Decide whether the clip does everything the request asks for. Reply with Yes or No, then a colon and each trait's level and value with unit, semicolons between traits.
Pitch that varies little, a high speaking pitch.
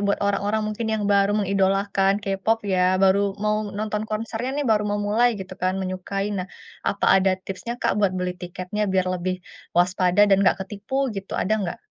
Yes: narrow, 2.1 semitones; high, 195 Hz